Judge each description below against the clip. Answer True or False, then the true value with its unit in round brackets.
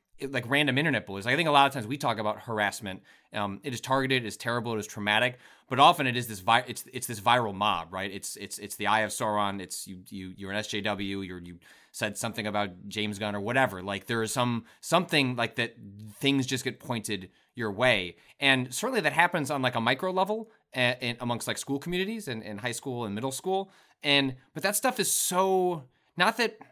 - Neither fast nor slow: False (225 wpm)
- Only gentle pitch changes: False (4.8 semitones)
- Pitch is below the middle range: True (120 Hz)